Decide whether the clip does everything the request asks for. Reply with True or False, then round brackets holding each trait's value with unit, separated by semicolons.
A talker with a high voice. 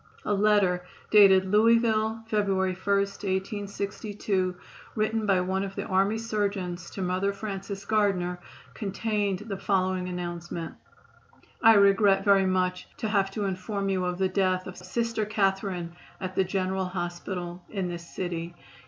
True (195 Hz)